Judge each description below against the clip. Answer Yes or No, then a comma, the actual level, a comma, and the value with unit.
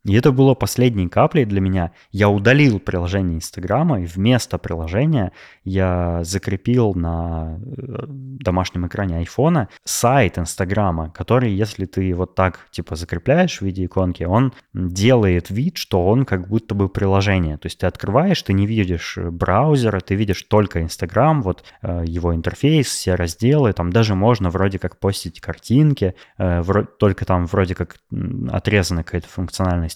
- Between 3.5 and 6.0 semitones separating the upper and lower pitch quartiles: Yes, average, 5.0 semitones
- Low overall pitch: Yes, very low, 95 Hz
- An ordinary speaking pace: Yes, average, 145 wpm